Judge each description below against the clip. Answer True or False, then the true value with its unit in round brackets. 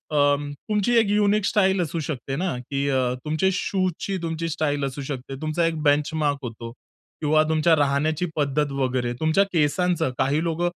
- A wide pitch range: False (3.7 semitones)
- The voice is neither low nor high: True (155 Hz)